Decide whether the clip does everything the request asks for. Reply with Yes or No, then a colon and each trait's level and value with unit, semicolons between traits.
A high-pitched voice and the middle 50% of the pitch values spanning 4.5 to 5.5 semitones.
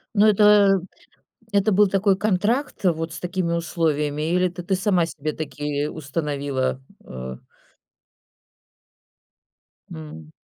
No: medium, 170 Hz; average, 4.9 semitones